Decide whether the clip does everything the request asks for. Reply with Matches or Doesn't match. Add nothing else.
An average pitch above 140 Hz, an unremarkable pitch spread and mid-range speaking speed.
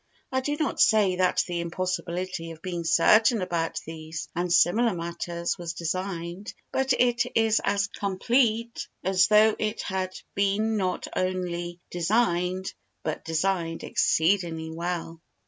Doesn't match